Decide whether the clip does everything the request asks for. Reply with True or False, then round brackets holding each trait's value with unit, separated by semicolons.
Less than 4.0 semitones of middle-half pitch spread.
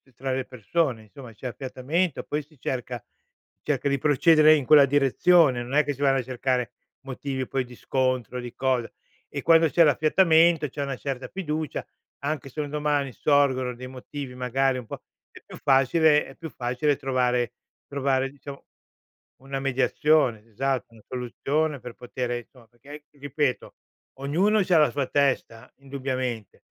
True (2.8 semitones)